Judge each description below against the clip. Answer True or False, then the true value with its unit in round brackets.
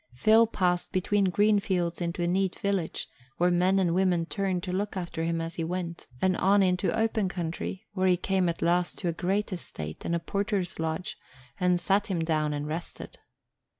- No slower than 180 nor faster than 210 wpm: True (195 wpm)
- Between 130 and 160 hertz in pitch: False (180 Hz)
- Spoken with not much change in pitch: True (2.3 semitones)